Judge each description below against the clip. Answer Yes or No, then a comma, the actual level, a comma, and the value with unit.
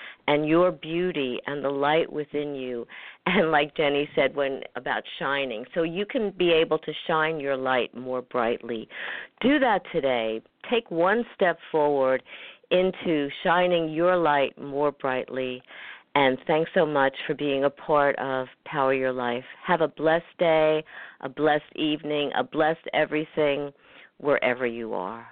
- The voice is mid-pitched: Yes, medium, 145 Hz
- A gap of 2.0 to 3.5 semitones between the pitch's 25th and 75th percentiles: Yes, average, 3.1 semitones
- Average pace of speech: Yes, average, 150 wpm